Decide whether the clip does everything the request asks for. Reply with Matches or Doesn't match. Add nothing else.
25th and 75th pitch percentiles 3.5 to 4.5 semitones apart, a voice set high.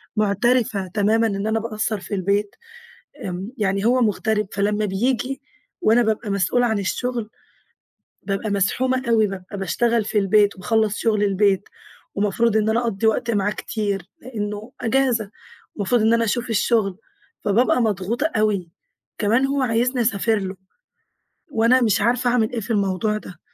Doesn't match